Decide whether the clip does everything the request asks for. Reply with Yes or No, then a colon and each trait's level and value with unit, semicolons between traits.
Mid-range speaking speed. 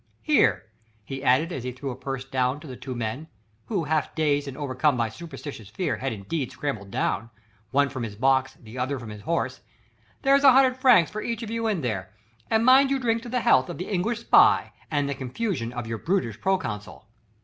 No: fast, 215 wpm